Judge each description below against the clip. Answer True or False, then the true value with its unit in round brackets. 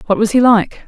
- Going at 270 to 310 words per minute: True (275 wpm)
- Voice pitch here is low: False (215 Hz)